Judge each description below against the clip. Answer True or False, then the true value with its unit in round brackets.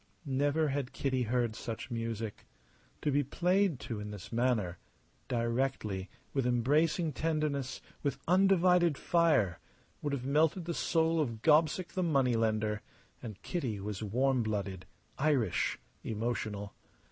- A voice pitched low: True (130 Hz)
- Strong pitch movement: True (5.8 semitones)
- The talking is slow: True (130 wpm)